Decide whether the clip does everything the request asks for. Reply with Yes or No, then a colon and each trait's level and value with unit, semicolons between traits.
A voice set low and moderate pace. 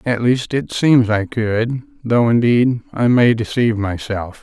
Yes: low, 120 Hz; average, 165 wpm